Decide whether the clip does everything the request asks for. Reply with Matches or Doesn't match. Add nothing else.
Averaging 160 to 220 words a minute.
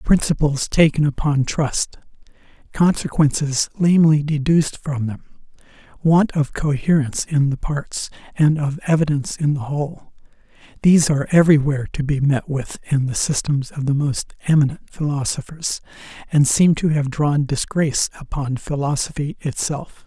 Doesn't match